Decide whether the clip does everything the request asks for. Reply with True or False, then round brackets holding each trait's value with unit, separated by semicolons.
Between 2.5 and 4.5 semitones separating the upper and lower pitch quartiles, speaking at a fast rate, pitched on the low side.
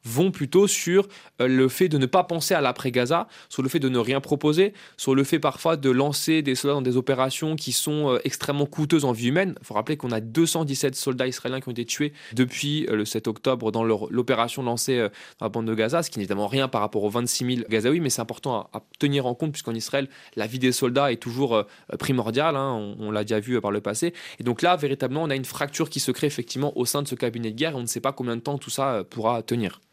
True (3.7 semitones; 260 wpm; 130 Hz)